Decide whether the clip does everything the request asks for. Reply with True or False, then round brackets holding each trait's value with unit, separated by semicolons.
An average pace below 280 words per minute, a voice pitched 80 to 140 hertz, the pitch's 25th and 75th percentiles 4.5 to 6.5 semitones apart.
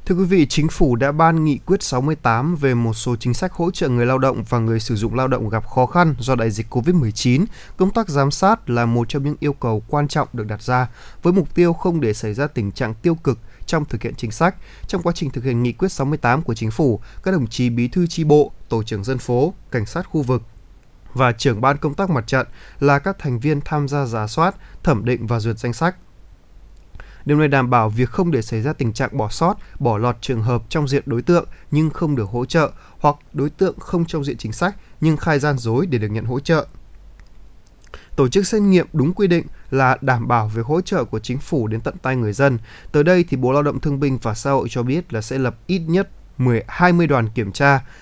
True (245 wpm; 135 Hz; 5.2 semitones)